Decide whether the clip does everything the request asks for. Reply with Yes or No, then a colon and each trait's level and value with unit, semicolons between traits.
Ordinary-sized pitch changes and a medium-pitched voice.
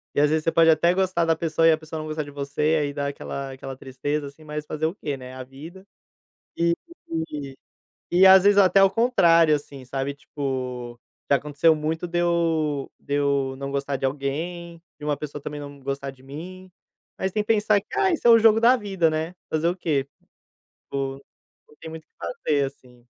Yes: average, 3.6 semitones; medium, 155 Hz